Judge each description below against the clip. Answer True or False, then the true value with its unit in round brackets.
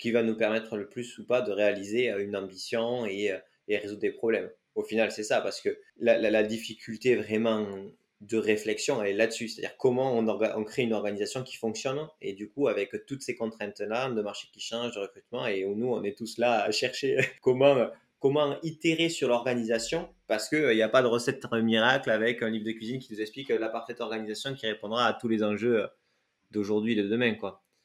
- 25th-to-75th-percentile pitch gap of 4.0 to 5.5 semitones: False (3.0 semitones)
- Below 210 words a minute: False (215 wpm)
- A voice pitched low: True (115 Hz)